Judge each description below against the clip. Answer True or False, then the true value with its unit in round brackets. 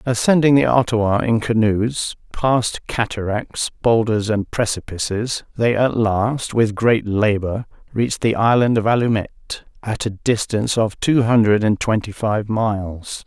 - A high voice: False (110 Hz)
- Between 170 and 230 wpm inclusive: False (140 wpm)